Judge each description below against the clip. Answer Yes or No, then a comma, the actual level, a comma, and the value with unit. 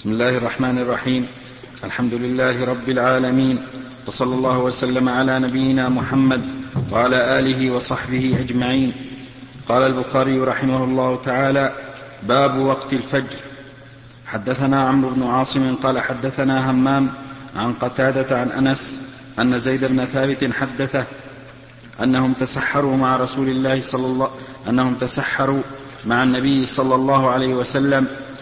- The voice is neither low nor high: No, low, 130 Hz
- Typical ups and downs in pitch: No, narrow, 1.0 semitones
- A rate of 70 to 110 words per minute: No, average, 120 wpm